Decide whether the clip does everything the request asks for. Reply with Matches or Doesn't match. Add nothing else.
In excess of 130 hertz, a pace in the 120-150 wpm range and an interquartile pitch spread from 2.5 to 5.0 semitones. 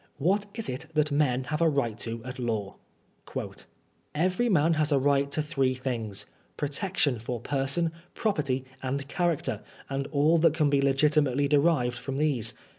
Doesn't match